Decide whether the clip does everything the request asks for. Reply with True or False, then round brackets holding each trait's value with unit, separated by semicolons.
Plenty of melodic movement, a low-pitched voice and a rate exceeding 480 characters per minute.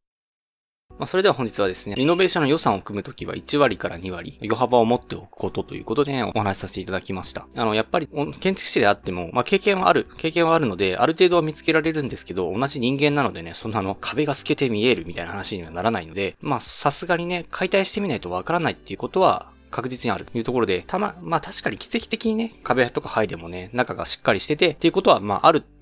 True (8.5 semitones; 125 Hz; 500 characters per minute)